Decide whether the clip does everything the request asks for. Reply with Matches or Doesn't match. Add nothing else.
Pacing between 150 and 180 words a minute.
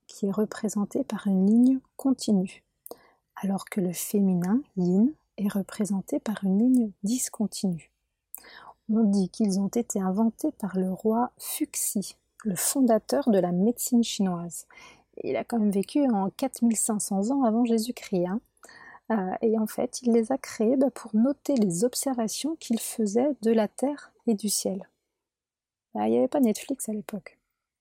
Matches